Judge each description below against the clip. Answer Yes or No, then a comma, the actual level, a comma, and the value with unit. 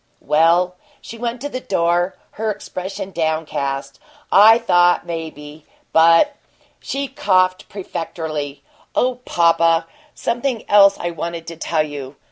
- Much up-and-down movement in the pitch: No, average, 4.0 semitones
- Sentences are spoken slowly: Yes, slow, 130 wpm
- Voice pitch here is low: No, medium, 175 Hz